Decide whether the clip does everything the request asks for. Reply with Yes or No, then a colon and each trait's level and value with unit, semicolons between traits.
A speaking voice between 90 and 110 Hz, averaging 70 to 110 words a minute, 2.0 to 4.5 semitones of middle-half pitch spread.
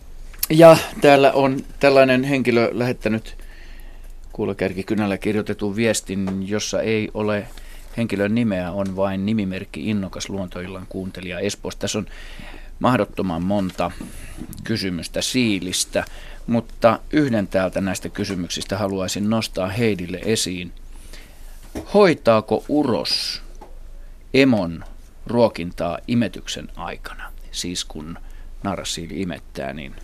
Yes: low, 100 Hz; slow, 95 wpm; average, 3.6 semitones